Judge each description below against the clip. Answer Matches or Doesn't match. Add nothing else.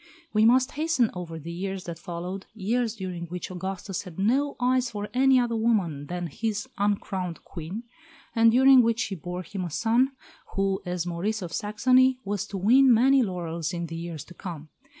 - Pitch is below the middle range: Doesn't match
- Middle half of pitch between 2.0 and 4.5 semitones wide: Doesn't match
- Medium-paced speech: Matches